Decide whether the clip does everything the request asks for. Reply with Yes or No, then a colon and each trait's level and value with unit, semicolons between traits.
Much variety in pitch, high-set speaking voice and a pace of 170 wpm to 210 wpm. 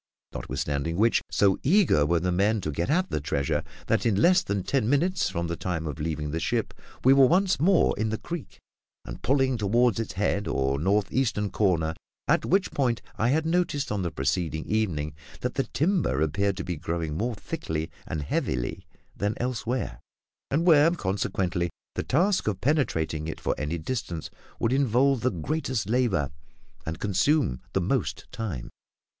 No: wide, 8.6 semitones; low, 105 Hz; average, 175 wpm